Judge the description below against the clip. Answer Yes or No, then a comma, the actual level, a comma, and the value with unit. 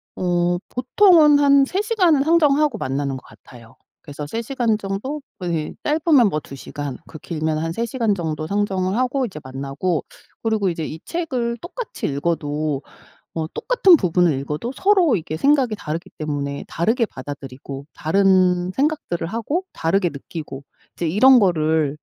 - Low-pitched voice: No, medium, 185 Hz